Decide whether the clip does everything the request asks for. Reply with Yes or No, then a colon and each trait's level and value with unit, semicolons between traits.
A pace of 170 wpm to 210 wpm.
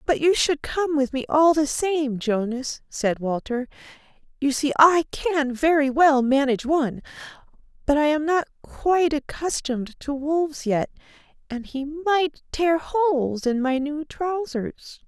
No: average, 150 wpm